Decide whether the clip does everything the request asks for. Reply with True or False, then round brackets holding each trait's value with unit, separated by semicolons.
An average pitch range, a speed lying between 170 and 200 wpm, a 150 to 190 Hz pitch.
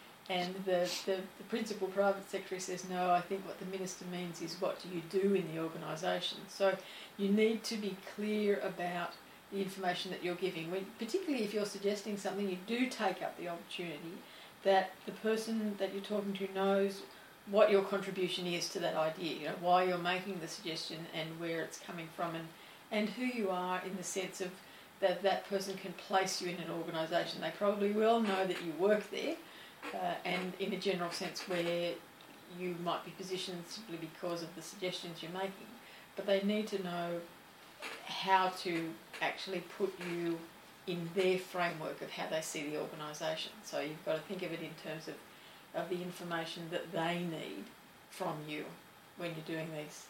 False (2.3 semitones; 190 wpm; 185 Hz)